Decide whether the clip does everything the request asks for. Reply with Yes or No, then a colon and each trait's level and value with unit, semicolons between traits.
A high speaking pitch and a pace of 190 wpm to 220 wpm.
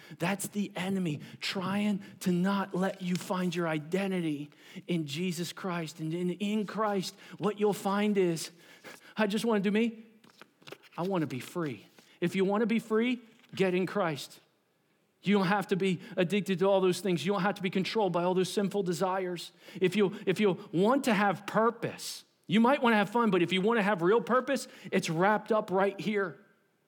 Yes: high, 195 Hz; average, 200 wpm